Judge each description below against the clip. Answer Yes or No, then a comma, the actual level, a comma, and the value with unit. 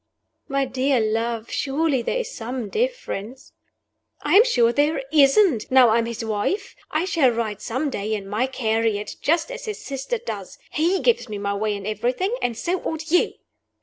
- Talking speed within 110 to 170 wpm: No, average, 180 wpm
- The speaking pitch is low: No, very high, 260 Hz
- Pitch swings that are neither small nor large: No, wide, 6.5 semitones